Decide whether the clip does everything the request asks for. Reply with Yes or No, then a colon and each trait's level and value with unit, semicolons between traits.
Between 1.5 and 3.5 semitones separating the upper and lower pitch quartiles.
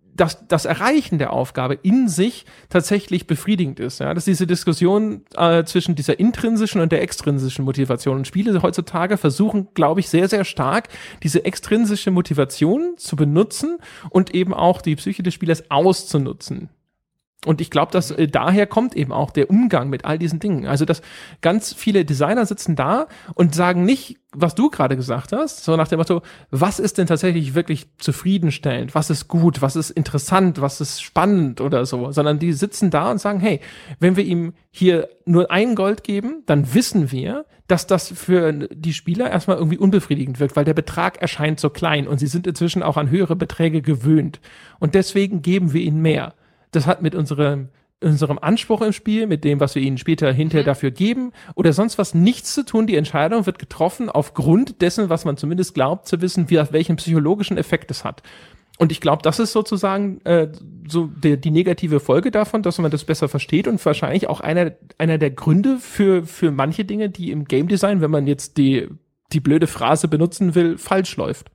No: average, 4.2 semitones